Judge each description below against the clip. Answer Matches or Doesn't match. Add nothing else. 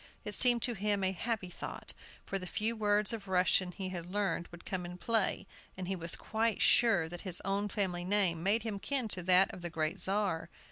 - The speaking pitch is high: Matches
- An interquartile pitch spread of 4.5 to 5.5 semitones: Doesn't match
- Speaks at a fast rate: Matches